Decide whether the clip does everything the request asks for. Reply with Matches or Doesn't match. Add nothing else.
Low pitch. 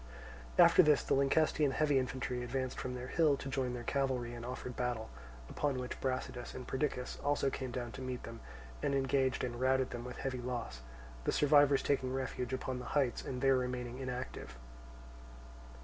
Matches